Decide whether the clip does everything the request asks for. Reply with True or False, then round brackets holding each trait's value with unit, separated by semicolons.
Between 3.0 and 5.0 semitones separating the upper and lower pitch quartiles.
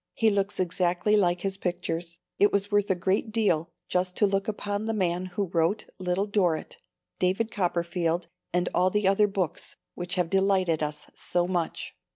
False (2.5 semitones)